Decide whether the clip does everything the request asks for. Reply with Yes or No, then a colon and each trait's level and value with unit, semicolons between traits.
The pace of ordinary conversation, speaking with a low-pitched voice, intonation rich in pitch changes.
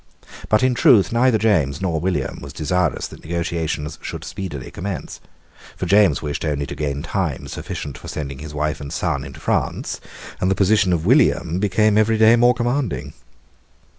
Yes: average, 170 wpm; very low, 90 Hz; wide, 6.1 semitones